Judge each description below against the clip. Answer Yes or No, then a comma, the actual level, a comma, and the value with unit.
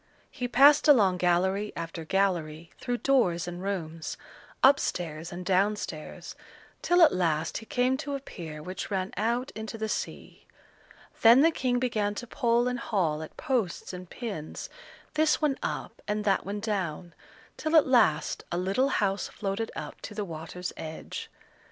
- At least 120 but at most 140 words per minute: No, average, 165 wpm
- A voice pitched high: Yes, high, 200 Hz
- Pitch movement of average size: No, wide, 5.9 semitones